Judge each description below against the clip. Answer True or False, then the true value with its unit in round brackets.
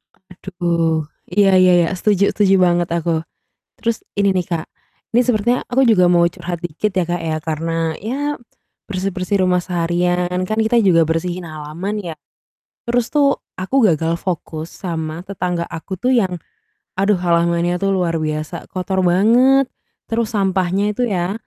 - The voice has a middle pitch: True (180 Hz)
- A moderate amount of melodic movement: True (3.0 semitones)